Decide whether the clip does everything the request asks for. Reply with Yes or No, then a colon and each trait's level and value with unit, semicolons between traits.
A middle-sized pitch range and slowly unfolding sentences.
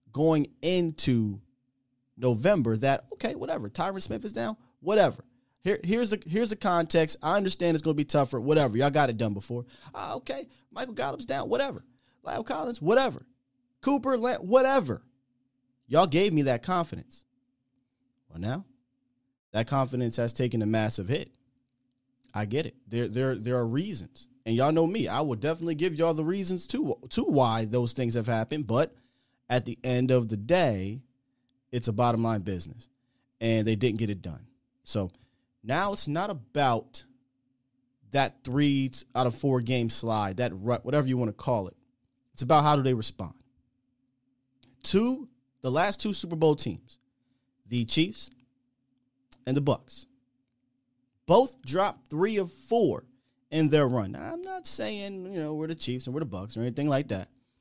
No: average, 3.7 semitones; average, 170 wpm